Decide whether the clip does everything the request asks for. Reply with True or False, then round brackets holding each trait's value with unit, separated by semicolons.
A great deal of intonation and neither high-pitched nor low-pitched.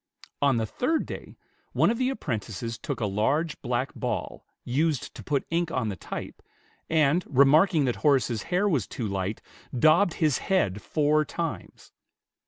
True (6.0 semitones; 145 Hz)